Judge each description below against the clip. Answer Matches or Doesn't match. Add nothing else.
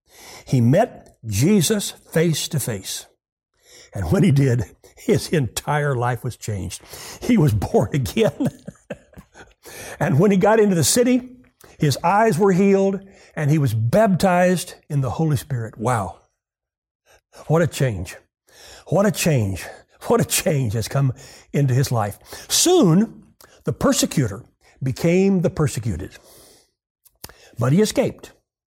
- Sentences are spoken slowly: Matches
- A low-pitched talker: Doesn't match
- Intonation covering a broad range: Matches